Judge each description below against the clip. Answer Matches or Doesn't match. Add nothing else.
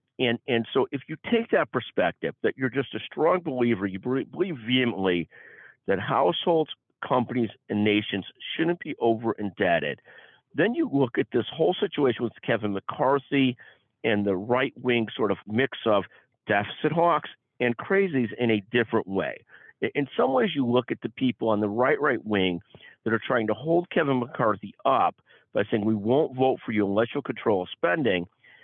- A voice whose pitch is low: Matches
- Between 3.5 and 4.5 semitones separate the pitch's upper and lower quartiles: Matches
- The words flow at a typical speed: Matches